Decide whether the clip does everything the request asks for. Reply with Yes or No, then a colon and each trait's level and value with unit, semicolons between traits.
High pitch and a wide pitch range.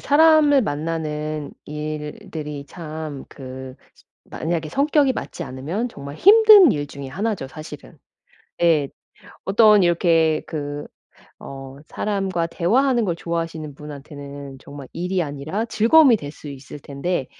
No: medium, 160 Hz; wide, 5.9 semitones